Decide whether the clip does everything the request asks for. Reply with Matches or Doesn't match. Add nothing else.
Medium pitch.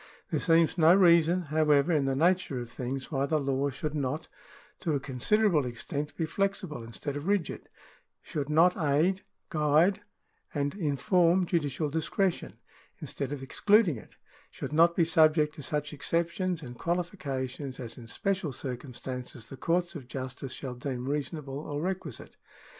Matches